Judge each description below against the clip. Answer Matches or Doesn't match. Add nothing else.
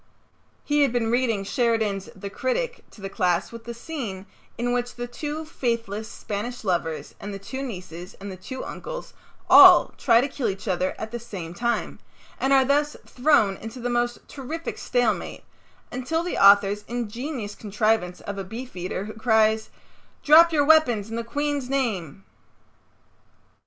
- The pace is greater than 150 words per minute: Matches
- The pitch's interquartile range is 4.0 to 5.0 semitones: Matches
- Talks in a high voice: Matches